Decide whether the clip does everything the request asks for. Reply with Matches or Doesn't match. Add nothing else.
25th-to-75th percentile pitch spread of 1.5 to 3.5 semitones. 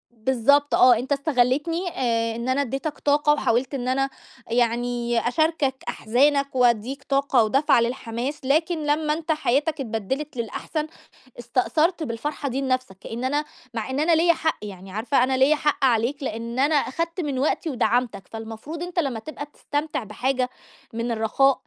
Doesn't match